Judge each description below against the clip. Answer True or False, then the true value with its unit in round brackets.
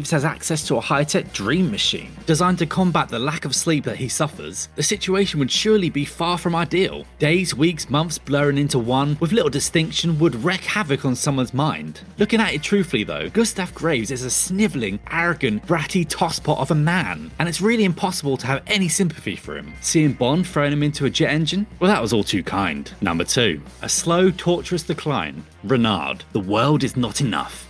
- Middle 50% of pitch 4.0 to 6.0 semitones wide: True (4.8 semitones)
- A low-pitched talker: False (160 Hz)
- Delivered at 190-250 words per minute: True (200 wpm)